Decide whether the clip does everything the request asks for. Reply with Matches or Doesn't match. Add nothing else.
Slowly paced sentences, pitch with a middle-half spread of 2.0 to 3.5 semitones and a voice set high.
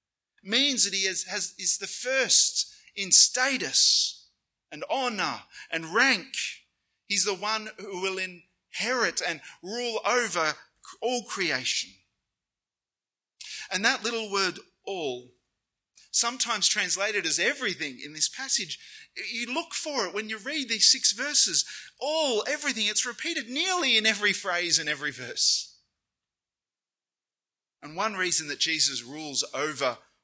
Doesn't match